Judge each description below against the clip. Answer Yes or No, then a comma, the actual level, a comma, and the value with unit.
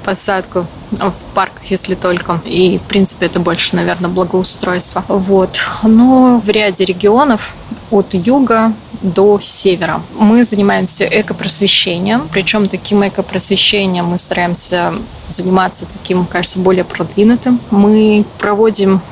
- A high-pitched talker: Yes, high, 195 Hz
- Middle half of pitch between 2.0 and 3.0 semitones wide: Yes, narrow, 2.5 semitones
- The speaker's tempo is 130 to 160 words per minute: No, average, 115 wpm